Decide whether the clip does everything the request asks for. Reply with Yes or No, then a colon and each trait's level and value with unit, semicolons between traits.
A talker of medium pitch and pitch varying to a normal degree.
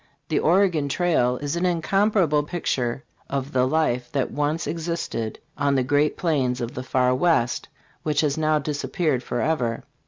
Yes: medium, 145 Hz; average, 4.4 semitones